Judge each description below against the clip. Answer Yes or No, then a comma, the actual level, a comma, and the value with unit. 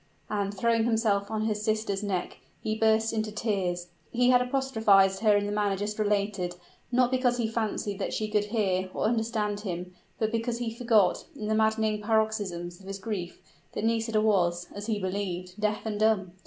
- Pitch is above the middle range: Yes, high, 210 Hz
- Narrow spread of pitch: Yes, narrow, 2.1 semitones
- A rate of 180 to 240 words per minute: Yes, average, 185 wpm